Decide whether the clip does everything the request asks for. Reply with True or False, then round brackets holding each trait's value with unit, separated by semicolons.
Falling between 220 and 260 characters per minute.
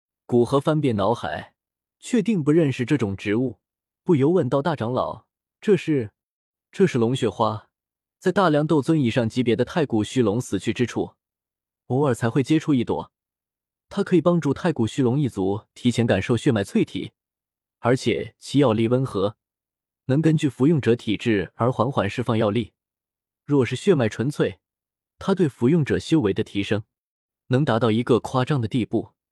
True (250 characters per minute)